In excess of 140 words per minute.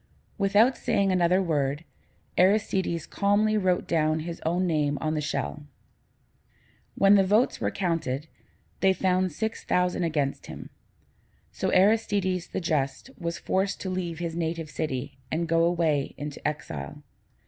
No: slow, 135 wpm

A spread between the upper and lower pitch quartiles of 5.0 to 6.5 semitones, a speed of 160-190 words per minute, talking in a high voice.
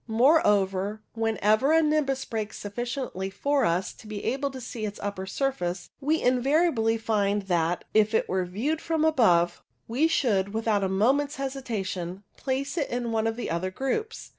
Yes: wide, 5.5 semitones; average, 165 wpm; high, 225 Hz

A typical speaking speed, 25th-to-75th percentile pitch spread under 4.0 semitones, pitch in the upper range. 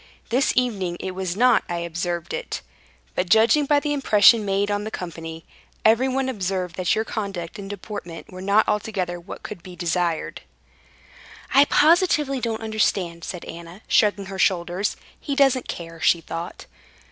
No: average, 155 wpm; average, 4.5 semitones; high, 195 Hz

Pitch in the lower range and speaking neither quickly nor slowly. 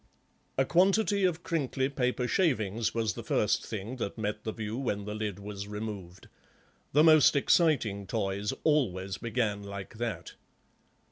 Yes: low, 110 Hz; average, 145 wpm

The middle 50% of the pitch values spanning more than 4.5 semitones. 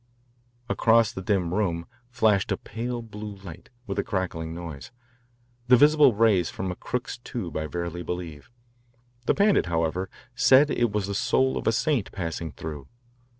Yes: wide, 5.5 semitones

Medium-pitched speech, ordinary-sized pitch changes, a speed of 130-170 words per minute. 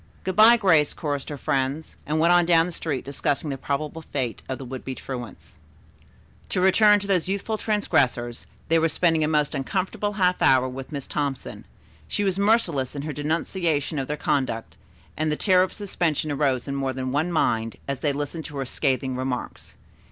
No: medium, 150 Hz; average, 4.7 semitones; average, 195 wpm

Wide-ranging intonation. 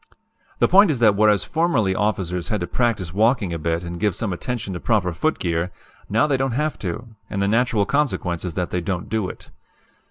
No: average, 5.0 semitones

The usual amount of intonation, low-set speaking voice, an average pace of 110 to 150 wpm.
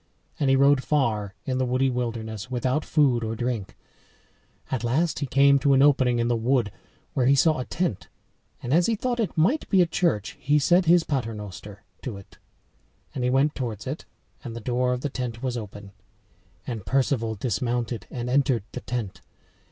No: average, 3.3 semitones; low, 125 Hz; average, 190 wpm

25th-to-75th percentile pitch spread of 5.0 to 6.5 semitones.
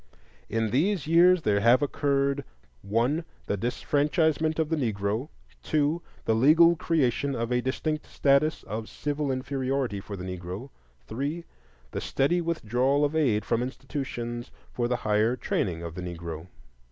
Yes: wide, 5.4 semitones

